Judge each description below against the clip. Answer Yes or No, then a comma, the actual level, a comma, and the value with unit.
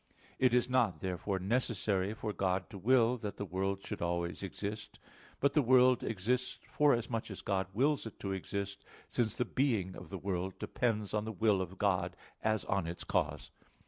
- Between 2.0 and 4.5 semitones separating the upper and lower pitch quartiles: Yes, average, 3.9 semitones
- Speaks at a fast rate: No, average, 180 wpm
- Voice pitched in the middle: No, low, 105 Hz